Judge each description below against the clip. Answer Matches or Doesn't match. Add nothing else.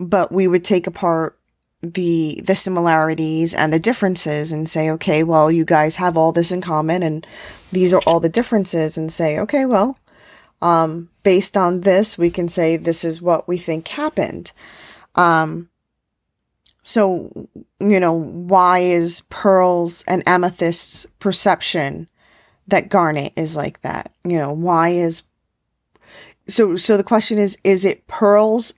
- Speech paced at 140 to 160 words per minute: Matches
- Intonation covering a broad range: Doesn't match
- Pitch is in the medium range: Matches